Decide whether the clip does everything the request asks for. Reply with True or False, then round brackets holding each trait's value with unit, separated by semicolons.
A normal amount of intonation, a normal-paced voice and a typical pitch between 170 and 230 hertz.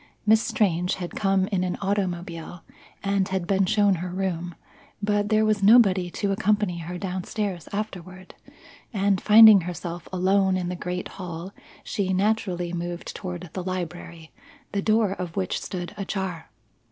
False (2.3 semitones; 155 wpm; 185 Hz)